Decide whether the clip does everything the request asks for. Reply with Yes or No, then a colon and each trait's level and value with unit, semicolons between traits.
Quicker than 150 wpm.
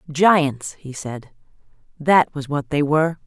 No: average, 145 wpm